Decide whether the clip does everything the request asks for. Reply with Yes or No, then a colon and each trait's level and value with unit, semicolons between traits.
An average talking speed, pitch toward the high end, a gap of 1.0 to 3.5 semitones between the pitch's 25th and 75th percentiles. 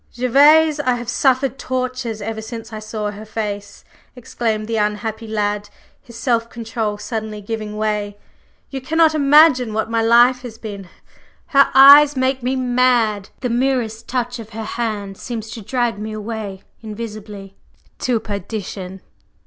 Yes: average, 150 wpm; high, 225 Hz; average, 3.0 semitones